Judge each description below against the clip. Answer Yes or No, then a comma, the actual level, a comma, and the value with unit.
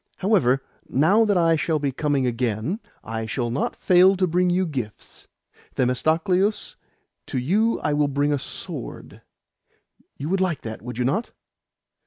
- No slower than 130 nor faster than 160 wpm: Yes, average, 155 wpm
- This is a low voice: No, medium, 150 Hz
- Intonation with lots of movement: Yes, wide, 6.5 semitones